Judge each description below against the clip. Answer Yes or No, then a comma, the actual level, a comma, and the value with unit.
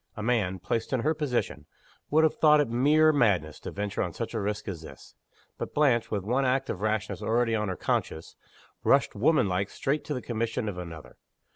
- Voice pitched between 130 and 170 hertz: No, low, 115 Hz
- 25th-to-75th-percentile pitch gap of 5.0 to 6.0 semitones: Yes, average, 5.3 semitones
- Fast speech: Yes, fast, 210 wpm